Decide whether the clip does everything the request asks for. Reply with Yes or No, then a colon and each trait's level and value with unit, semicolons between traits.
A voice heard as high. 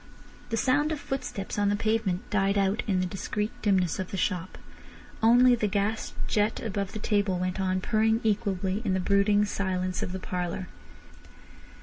Yes: high, 200 Hz